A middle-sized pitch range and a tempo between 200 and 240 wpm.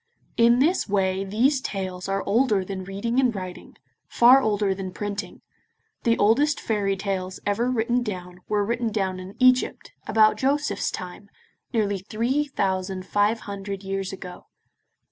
No: average, 3.5 semitones; average, 145 wpm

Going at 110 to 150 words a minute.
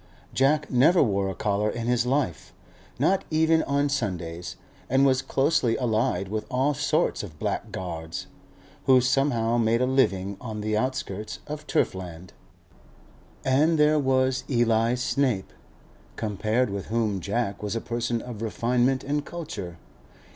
Yes: average, 140 wpm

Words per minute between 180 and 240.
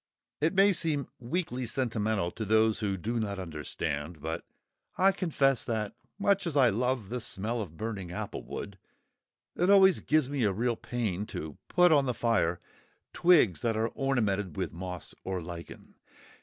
No: average, 160 wpm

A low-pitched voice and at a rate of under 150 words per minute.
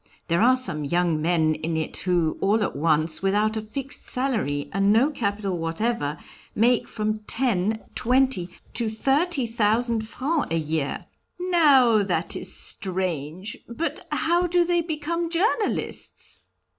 No: high, 215 Hz; average, 140 wpm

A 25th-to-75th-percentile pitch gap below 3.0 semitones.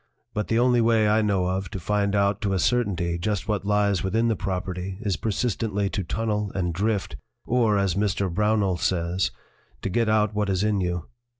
Yes: narrow, 2.4 semitones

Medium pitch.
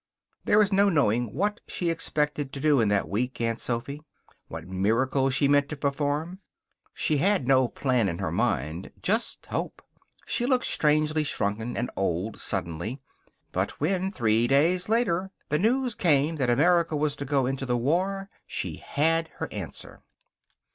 Yes: medium, 145 Hz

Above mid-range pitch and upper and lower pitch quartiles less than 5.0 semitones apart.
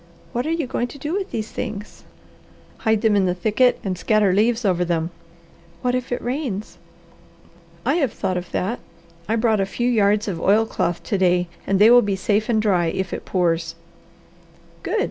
Yes: high, 210 Hz; average, 4.4 semitones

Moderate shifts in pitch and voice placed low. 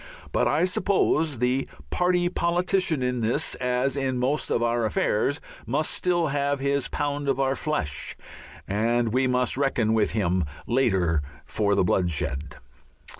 Yes: average, 4.5 semitones; low, 130 Hz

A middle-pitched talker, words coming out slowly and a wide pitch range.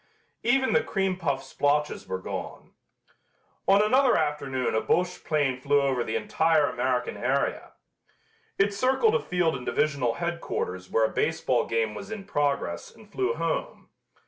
No: medium, 150 Hz; average, 150 wpm; wide, 7.4 semitones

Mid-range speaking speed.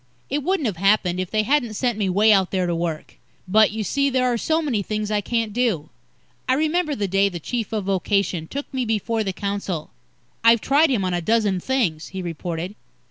No: fast, 215 wpm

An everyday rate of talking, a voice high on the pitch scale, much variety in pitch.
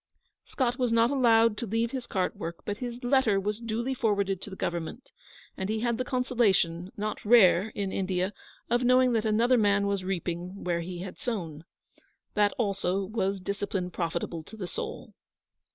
No: average, 175 wpm; high, 205 Hz; average, 4.0 semitones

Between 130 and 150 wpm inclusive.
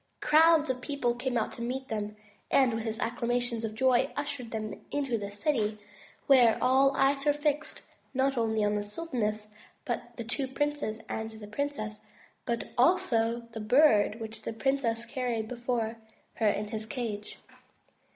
No: average, 160 wpm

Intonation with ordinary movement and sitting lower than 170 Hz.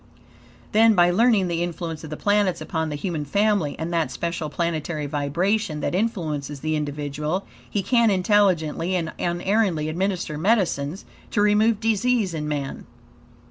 No: average, 5.0 semitones; medium, 175 Hz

